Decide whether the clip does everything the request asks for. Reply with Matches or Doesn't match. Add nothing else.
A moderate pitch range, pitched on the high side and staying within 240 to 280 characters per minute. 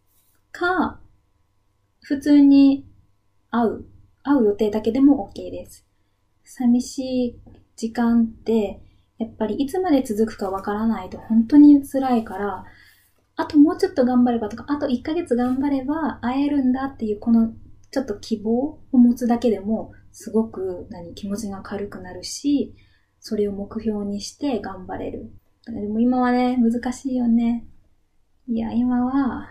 Matches